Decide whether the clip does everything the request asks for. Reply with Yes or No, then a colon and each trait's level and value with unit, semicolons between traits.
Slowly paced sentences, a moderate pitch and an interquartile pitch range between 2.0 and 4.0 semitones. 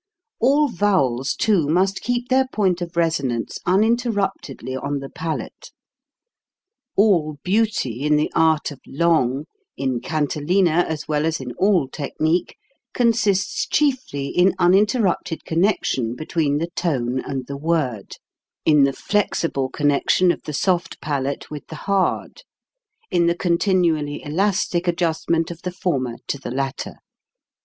No: slow, 130 wpm; medium, 165 Hz; average, 5.1 semitones